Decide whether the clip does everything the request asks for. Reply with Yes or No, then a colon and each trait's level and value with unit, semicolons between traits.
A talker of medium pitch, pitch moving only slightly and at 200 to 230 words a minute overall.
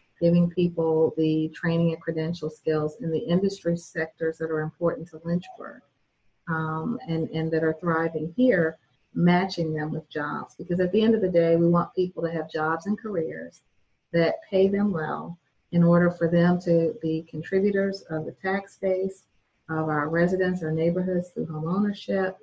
No: medium, 170 Hz; narrow, 2.3 semitones; average, 175 wpm